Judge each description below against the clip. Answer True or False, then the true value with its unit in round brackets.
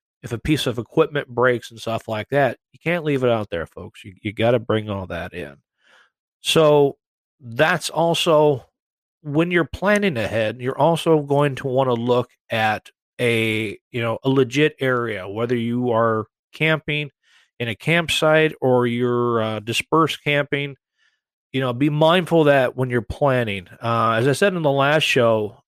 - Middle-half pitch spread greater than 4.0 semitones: True (4.7 semitones)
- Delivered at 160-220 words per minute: True (175 wpm)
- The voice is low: True (130 Hz)